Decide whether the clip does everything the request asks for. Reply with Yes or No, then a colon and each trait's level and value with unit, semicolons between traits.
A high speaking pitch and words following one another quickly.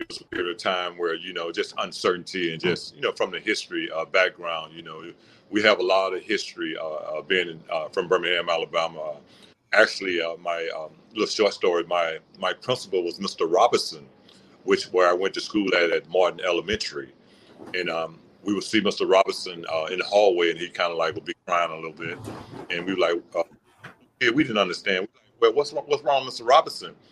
Yes: very high, 355 Hz; fast, 210 wpm